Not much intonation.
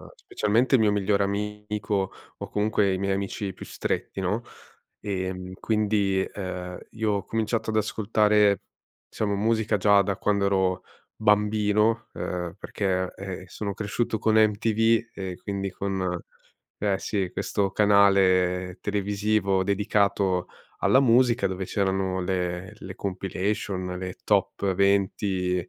Yes: narrow, 2.0 semitones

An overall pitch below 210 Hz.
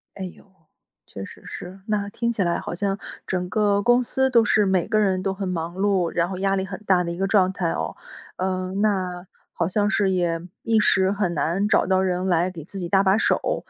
Yes: high, 190 Hz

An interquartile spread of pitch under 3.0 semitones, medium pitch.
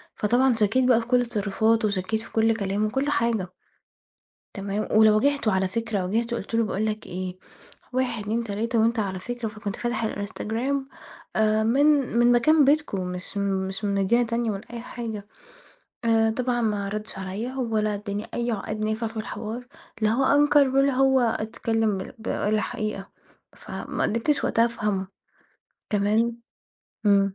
No: narrow, 2.6 semitones; high, 220 Hz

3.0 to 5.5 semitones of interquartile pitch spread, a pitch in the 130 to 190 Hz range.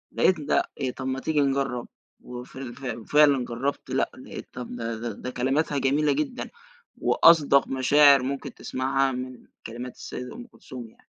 No: narrow, 2.4 semitones; low, 135 Hz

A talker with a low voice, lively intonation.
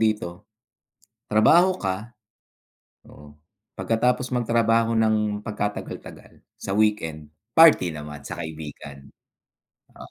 Yes: low, 105 Hz; wide, 6.2 semitones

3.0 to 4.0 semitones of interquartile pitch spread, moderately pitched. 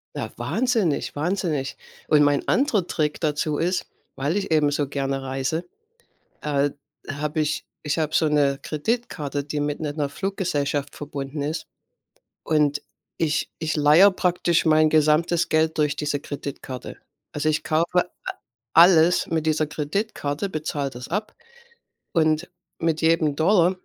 No: narrow, 2.5 semitones; medium, 155 Hz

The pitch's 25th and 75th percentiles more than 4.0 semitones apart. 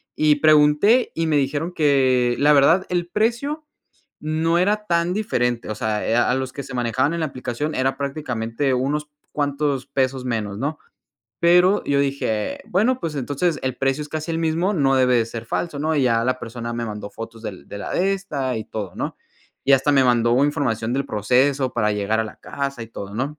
Yes: average, 4.6 semitones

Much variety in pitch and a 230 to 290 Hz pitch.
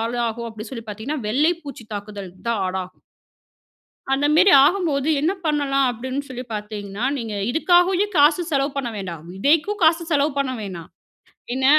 Yes: wide, 5.8 semitones; very high, 260 Hz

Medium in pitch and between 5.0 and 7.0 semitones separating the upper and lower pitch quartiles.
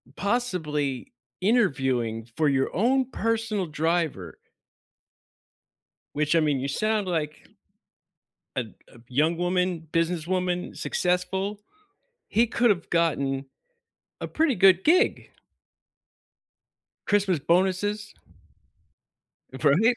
Yes: medium, 180 Hz; wide, 5.4 semitones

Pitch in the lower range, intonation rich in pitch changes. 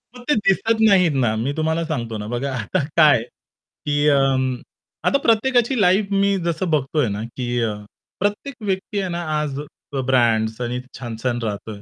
No: medium, 145 Hz; wide, 7.9 semitones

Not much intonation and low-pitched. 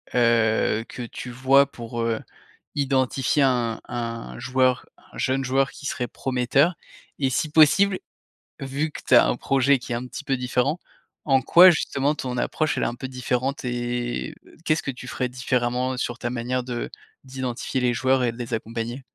Yes: narrow, 2.0 semitones; low, 125 Hz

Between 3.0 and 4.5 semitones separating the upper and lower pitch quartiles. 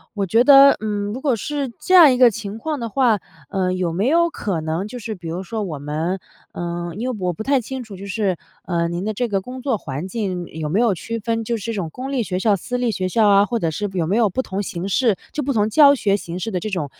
No: average, 4.9 semitones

